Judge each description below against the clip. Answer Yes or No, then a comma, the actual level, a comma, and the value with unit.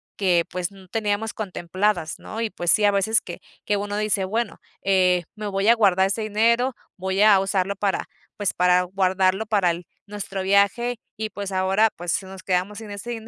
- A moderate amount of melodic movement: No, narrow, 2.3 semitones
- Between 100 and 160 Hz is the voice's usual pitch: No, high, 200 Hz